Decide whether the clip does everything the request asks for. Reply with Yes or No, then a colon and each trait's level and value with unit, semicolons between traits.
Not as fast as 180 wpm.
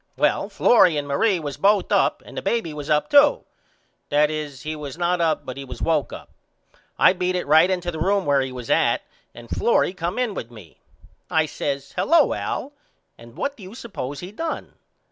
No: average, 200 wpm